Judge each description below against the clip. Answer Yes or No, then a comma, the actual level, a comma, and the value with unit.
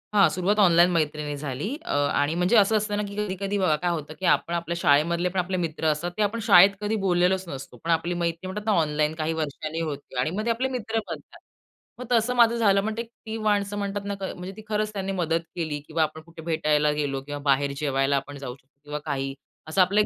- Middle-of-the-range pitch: Yes, medium, 170 Hz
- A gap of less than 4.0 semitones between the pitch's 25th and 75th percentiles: No, average, 5.1 semitones